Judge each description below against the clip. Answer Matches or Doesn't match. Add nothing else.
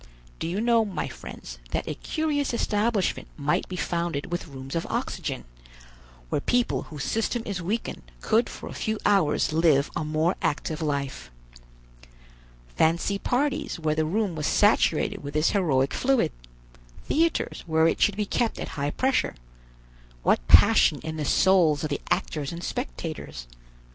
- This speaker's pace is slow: Doesn't match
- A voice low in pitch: Doesn't match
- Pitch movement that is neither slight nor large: Doesn't match